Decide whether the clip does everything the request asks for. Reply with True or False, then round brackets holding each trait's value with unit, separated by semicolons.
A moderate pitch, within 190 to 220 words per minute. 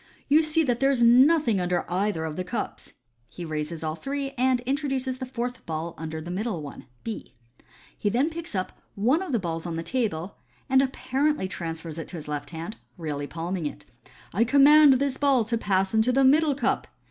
False (225 Hz; 205 wpm)